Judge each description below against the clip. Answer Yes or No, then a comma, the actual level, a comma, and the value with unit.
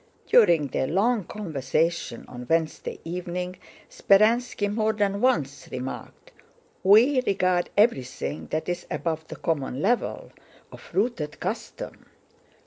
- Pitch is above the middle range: No, medium, 180 Hz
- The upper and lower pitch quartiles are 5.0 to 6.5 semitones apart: Yes, wide, 5.4 semitones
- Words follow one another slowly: Yes, slow, 115 wpm